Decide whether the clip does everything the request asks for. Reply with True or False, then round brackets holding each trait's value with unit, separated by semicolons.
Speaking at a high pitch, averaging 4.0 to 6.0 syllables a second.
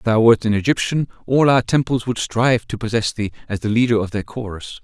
False (115 Hz; 5.9 syllables/s)